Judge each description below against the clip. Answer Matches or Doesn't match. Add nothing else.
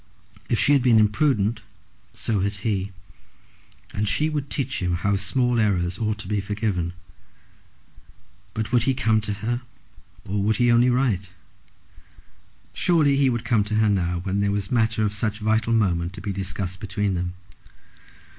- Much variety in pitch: Doesn't match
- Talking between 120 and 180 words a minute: Matches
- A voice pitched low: Matches